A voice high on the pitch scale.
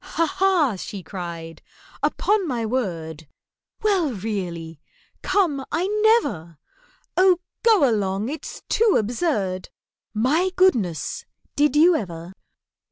Yes: high, 235 Hz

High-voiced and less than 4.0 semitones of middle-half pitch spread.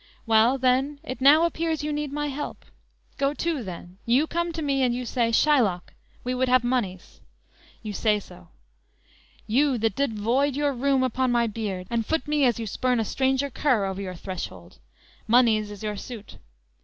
No: very high, 250 Hz; average, 4.4 semitones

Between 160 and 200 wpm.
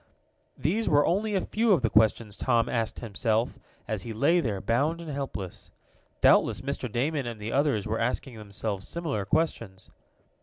Yes: average, 165 wpm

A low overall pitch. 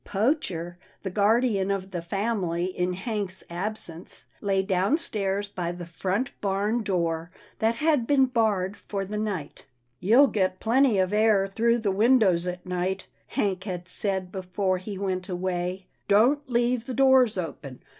No: high, 195 Hz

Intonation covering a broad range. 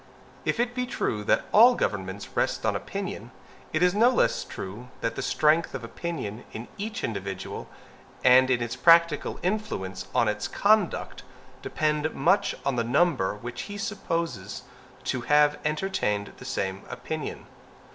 Yes: wide, 8.2 semitones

